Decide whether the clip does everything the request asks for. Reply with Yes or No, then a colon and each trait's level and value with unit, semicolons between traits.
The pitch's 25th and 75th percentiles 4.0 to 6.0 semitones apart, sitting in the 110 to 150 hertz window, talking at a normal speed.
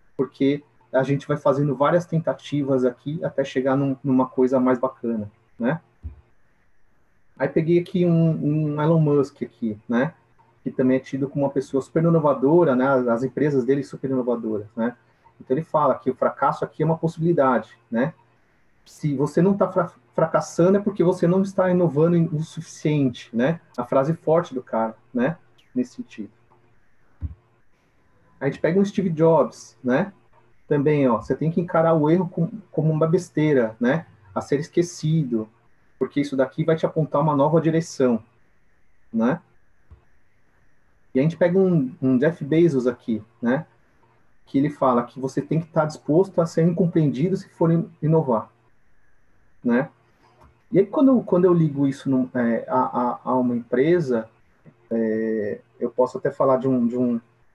Yes: average, 5.0 semitones; medium, 140 Hz; average, 165 wpm